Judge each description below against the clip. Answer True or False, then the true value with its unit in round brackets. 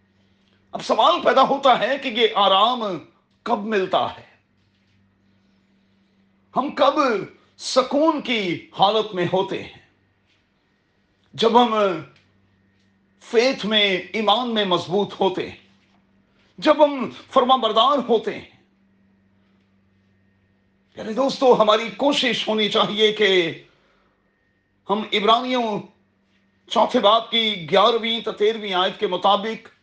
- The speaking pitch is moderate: False (195 Hz)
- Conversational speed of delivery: False (105 wpm)